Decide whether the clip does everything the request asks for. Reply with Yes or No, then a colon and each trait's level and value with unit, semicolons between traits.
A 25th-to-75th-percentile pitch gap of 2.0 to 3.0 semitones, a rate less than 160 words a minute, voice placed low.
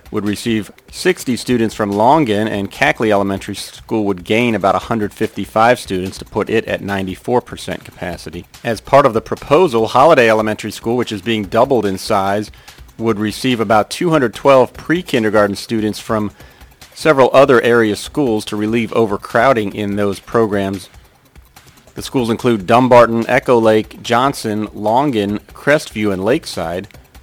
Yes: average, 2.7 semitones; average, 140 wpm; low, 110 Hz